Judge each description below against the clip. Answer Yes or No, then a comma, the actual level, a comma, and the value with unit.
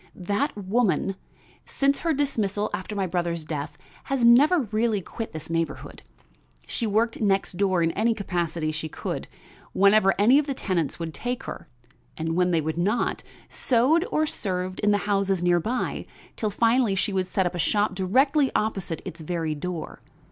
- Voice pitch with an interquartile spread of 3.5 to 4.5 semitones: No, average, 4.9 semitones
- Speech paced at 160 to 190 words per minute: Yes, average, 170 wpm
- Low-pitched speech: No, high, 195 Hz